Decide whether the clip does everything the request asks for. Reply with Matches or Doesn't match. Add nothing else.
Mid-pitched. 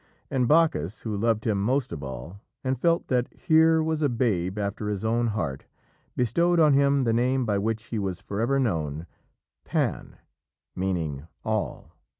Doesn't match